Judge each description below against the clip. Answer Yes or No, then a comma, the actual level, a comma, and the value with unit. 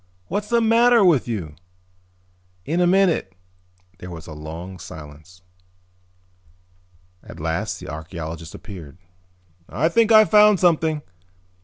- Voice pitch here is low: Yes, low, 105 Hz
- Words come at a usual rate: No, slow, 120 wpm